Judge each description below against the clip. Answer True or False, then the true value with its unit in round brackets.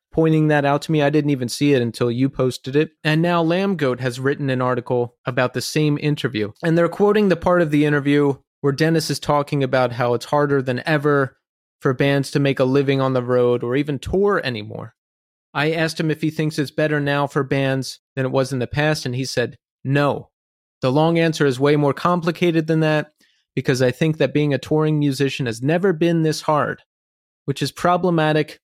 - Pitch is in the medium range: True (145 Hz)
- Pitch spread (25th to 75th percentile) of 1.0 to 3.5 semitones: True (3.0 semitones)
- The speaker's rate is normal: False (215 wpm)